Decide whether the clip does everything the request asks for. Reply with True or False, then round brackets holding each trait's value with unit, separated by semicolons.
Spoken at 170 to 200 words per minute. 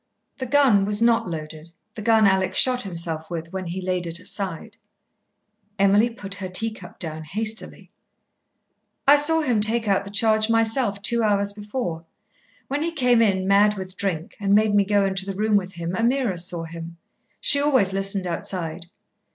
True (175 wpm)